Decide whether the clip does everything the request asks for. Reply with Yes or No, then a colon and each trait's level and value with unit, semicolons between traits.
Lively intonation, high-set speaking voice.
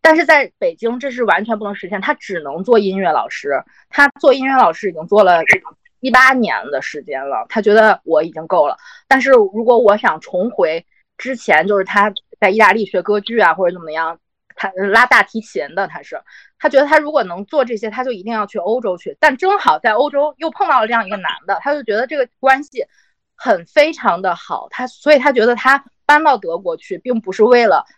Yes: wide, 6.0 semitones; very high, 250 Hz